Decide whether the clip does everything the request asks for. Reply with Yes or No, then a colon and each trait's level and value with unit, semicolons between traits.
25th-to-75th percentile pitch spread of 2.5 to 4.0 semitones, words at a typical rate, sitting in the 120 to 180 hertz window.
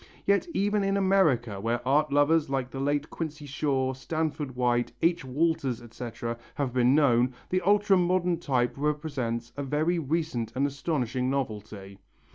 No: average, 4.7 semitones; average, 150 wpm; medium, 140 Hz